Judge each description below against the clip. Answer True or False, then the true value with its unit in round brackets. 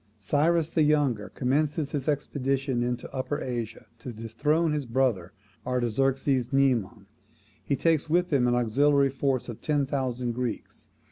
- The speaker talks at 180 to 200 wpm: False (140 wpm)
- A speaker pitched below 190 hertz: True (135 Hz)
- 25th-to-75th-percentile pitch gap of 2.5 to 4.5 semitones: True (3.2 semitones)